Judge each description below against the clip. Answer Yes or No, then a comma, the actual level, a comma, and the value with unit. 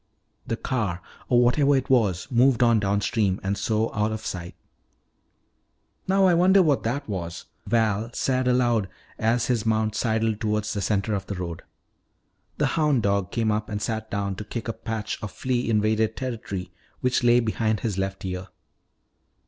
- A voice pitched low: Yes, low, 110 Hz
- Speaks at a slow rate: No, average, 170 wpm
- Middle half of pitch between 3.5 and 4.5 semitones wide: No, average, 3.1 semitones